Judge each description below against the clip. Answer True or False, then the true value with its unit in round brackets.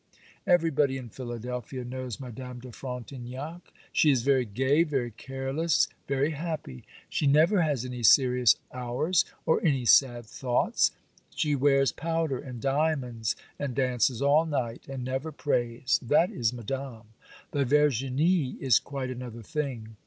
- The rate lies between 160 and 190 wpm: False (135 wpm)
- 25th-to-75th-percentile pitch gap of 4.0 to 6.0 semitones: False (3.0 semitones)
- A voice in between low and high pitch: False (130 Hz)